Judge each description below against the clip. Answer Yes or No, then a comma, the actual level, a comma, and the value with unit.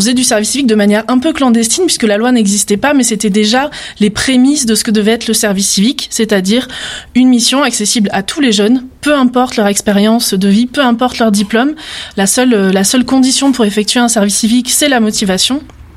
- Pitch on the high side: Yes, high, 235 Hz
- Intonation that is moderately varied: Yes, average, 3.3 semitones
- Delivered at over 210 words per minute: Yes, fast, 220 wpm